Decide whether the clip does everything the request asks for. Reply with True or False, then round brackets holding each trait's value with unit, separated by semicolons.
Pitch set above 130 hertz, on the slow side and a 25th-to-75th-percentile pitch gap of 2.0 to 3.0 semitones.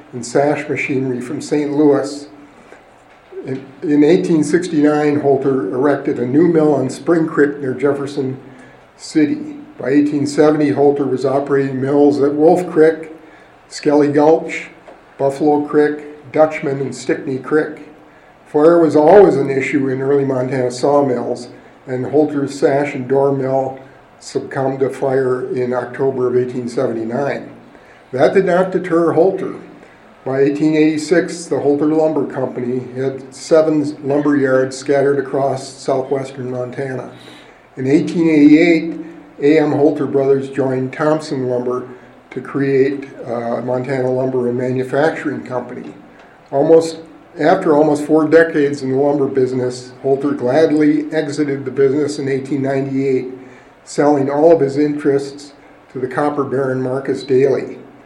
True (140 Hz; 125 wpm; 2.4 semitones)